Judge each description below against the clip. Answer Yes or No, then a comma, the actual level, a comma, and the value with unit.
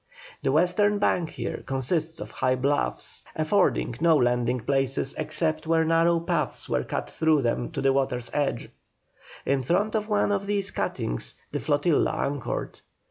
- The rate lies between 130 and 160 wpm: Yes, average, 155 wpm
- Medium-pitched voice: Yes, medium, 155 Hz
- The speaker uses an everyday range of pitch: Yes, average, 4.3 semitones